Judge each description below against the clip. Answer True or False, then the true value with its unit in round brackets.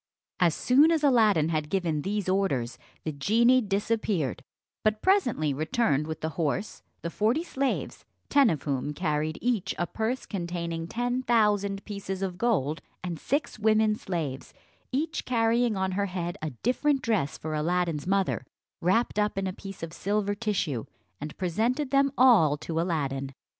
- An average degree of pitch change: False (6.3 semitones)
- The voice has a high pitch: True (195 Hz)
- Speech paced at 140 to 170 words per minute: True (160 wpm)